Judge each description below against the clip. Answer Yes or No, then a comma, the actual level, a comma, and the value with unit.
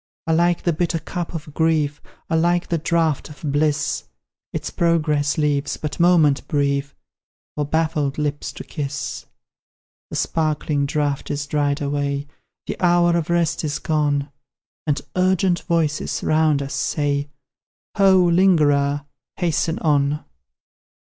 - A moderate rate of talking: No, slow, 125 wpm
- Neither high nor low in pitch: Yes, medium, 150 Hz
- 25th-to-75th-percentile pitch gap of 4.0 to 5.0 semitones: No, narrow, 2.6 semitones